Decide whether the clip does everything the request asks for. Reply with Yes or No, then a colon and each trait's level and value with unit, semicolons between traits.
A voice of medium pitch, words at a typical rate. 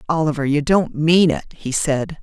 Yes: medium, 155 Hz; average, 190 wpm